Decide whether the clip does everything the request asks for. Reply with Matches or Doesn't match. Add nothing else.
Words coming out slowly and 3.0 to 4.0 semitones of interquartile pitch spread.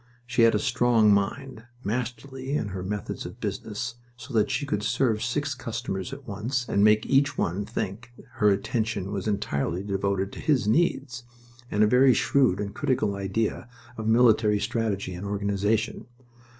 Doesn't match